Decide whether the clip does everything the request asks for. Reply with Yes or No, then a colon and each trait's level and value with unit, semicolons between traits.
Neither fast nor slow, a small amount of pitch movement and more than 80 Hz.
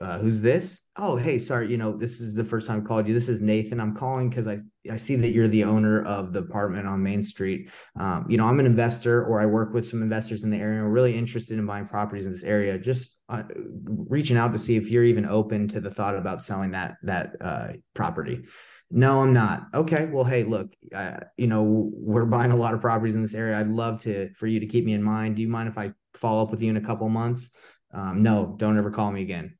No: fast, 255 wpm; narrow, 1.8 semitones; low, 110 Hz